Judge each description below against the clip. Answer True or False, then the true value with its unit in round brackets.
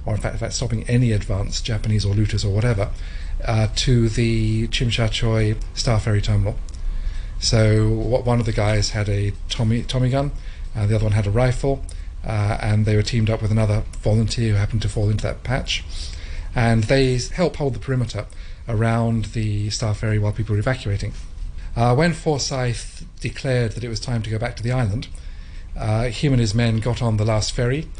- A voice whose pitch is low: True (110 Hz)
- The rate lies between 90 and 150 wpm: False (200 wpm)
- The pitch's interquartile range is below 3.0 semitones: True (2.6 semitones)